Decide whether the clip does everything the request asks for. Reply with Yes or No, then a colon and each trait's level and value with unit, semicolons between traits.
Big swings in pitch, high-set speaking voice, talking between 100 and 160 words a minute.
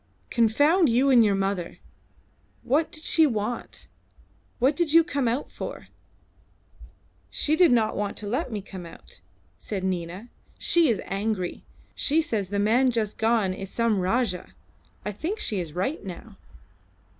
Yes: wide, 6.0 semitones; high, 225 Hz; average, 155 wpm